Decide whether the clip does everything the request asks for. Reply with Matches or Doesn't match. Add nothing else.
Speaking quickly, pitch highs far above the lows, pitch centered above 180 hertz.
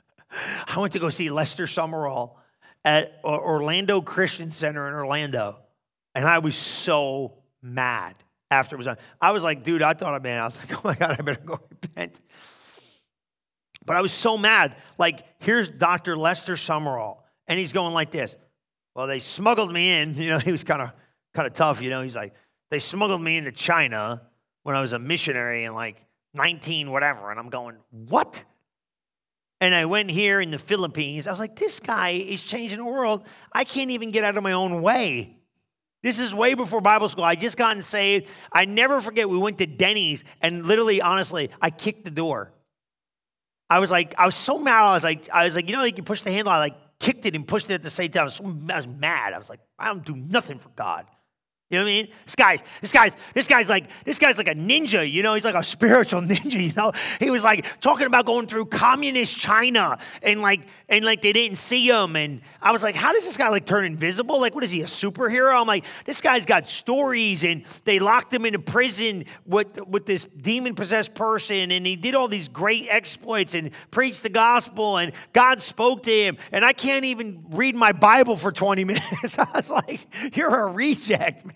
Matches